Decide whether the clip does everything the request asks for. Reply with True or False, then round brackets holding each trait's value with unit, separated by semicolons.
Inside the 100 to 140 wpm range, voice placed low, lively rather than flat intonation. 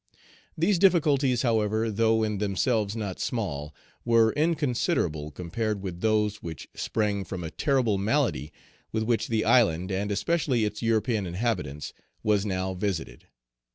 False (135 wpm; 110 Hz; 3.6 semitones)